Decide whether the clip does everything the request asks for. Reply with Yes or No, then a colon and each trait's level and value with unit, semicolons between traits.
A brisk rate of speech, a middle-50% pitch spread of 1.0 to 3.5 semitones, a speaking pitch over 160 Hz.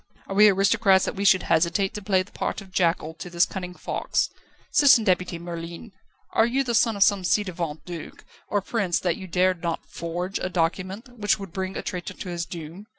Yes: fast, 210 wpm; average, 2.7 semitones; medium, 185 Hz